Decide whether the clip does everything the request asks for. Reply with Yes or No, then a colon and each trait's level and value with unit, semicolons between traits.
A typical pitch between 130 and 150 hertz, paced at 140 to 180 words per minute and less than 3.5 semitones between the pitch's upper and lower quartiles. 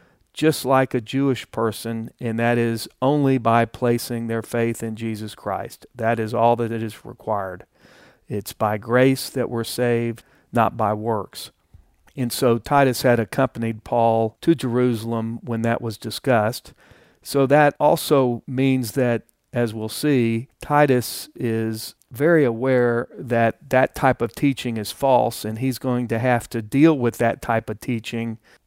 No: low, 120 Hz; average, 155 wpm; narrow, 2.4 semitones